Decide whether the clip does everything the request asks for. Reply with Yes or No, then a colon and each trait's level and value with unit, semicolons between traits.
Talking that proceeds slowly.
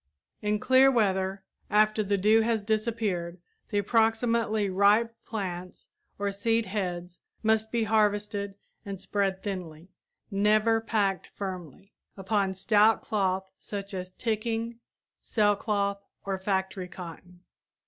Yes: slow, 115 wpm